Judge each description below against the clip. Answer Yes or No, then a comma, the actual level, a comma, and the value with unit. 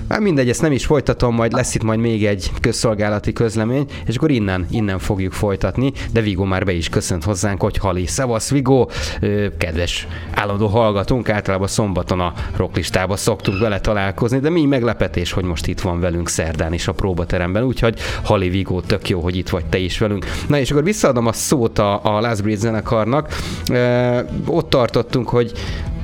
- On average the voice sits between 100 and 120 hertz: Yes, low, 105 Hz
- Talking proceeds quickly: Yes, fast, 180 wpm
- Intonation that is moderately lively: Yes, average, 4.2 semitones